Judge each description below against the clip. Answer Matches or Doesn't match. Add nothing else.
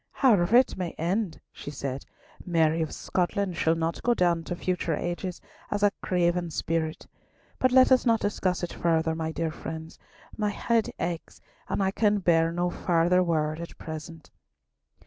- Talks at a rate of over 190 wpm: Doesn't match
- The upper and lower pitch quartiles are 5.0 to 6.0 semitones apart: Doesn't match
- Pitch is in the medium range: Matches